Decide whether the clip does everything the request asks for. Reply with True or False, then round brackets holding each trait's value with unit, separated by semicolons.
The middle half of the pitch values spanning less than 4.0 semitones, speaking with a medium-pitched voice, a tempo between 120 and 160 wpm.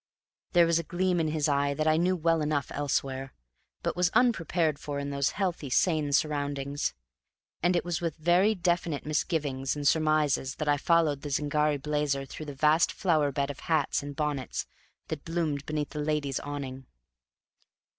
False (2.7 semitones; 150 Hz; 175 wpm)